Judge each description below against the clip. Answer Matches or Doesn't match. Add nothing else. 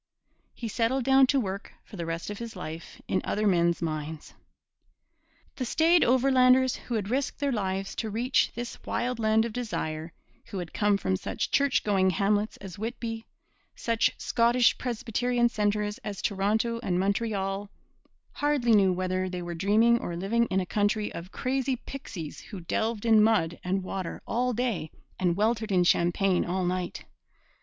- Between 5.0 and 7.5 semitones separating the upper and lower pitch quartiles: Doesn't match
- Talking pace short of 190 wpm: Matches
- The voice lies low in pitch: Doesn't match